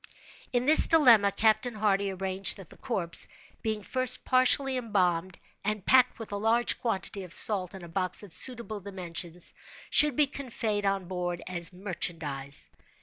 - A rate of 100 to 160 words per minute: Yes, average, 155 wpm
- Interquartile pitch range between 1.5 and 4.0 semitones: No, average, 4.4 semitones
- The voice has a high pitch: Yes, high, 200 Hz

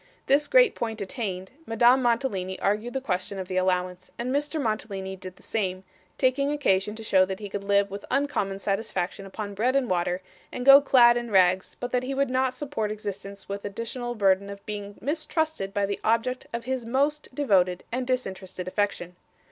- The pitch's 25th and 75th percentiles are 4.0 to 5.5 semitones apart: Yes, average, 4.8 semitones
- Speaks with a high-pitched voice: Yes, high, 215 Hz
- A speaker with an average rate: Yes, average, 190 wpm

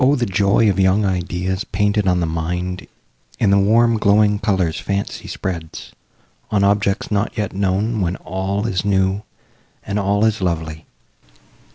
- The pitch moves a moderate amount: No, narrow, 2.1 semitones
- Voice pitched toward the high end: No, low, 100 Hz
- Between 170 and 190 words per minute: No, average, 150 wpm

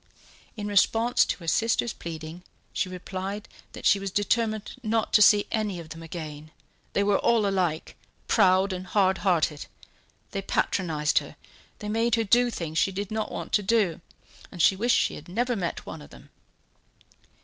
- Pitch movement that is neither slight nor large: Yes, average, 3.8 semitones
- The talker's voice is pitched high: Yes, high, 195 Hz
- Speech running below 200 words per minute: Yes, average, 175 wpm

